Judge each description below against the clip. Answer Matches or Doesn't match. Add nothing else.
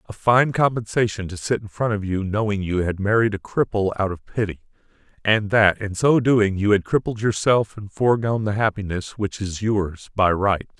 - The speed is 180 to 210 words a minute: Matches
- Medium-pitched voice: Doesn't match